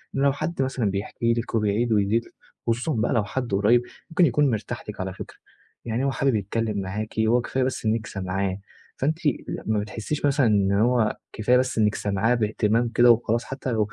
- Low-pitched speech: Yes, low, 115 Hz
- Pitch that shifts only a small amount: No, average, 3.1 semitones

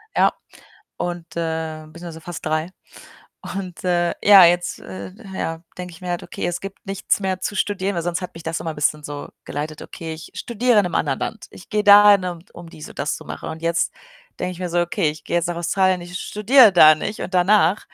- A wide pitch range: No, average, 2.8 semitones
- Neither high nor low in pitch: Yes, medium, 175 Hz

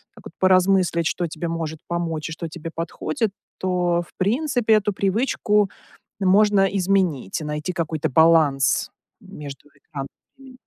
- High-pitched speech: No, medium, 175 Hz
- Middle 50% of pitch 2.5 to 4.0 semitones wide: Yes, average, 3.7 semitones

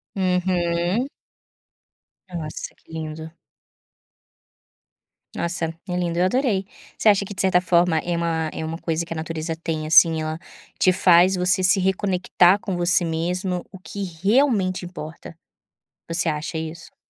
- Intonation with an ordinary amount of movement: No, narrow, 2.3 semitones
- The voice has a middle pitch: Yes, medium, 175 Hz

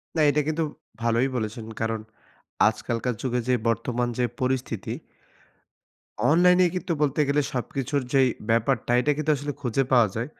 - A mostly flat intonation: No, average, 3.9 semitones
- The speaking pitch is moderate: No, low, 130 Hz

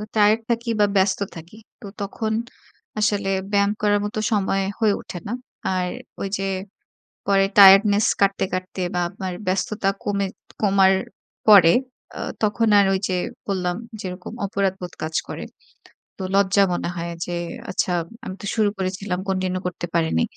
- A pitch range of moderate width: No, narrow, 1.9 semitones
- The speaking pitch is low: No, high, 195 Hz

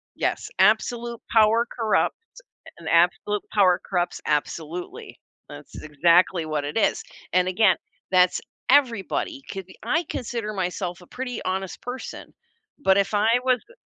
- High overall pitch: Yes, high, 195 Hz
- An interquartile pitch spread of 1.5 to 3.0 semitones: No, average, 4.8 semitones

